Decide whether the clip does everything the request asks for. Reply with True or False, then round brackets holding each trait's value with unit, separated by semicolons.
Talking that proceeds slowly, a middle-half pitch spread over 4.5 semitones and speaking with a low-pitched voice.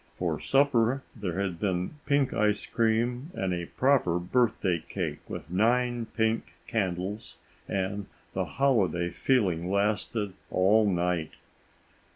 True (120 wpm; 4.9 semitones; 105 Hz)